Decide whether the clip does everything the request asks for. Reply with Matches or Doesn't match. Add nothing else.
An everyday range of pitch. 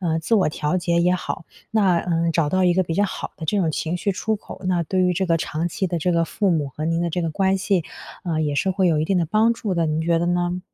Doesn't match